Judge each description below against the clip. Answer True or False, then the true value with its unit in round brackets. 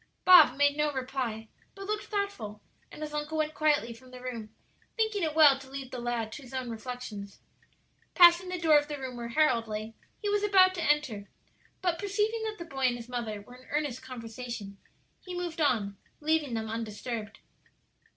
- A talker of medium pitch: False (265 Hz)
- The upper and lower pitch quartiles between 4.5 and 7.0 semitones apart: True (5.5 semitones)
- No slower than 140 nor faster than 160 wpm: False (195 wpm)